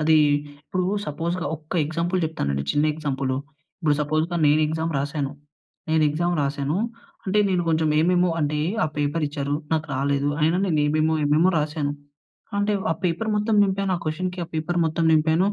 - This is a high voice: No, medium, 155 Hz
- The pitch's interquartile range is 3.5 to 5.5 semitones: No, average, 2.9 semitones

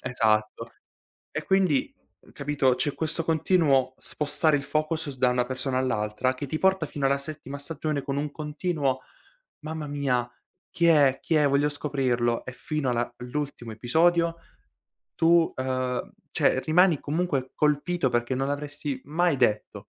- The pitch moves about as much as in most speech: Yes, average, 3.4 semitones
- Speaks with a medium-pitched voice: Yes, medium, 145 Hz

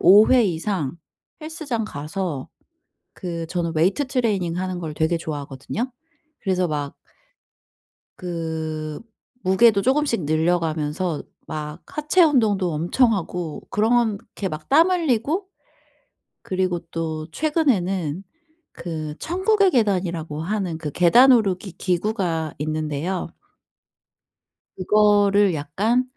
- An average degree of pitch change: No, wide, 5.7 semitones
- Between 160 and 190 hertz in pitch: Yes, medium, 185 Hz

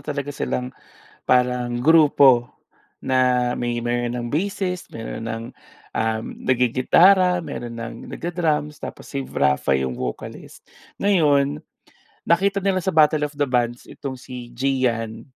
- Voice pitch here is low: Yes, low, 130 Hz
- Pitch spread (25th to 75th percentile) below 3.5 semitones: No, average, 4.3 semitones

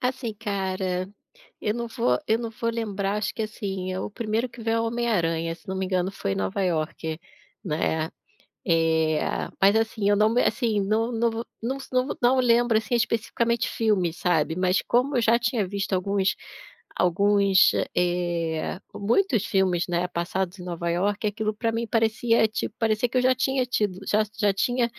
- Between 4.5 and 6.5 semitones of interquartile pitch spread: No, average, 4.0 semitones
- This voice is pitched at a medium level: No, high, 210 Hz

